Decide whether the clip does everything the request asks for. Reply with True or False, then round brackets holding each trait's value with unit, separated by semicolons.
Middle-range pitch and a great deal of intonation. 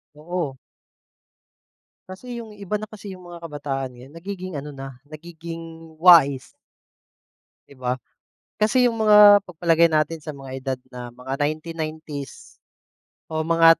False (165 Hz; 4.5 semitones)